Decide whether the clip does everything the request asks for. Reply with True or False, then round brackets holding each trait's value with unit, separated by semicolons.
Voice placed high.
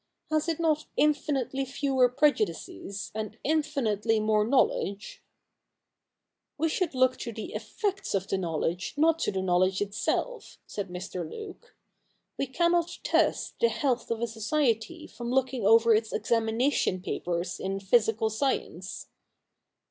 True (235 Hz)